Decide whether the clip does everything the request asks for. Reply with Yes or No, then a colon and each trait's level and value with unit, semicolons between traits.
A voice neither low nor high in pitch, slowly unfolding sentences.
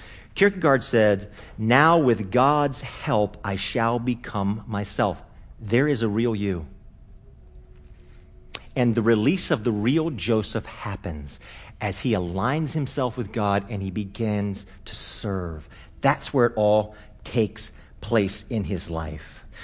No: low, 105 Hz; slow, 130 wpm